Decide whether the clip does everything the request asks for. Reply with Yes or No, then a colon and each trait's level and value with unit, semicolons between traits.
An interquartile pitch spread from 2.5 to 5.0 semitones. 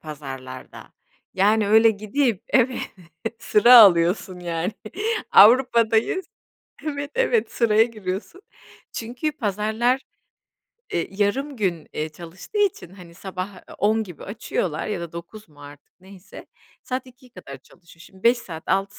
No: wide, 5.4 semitones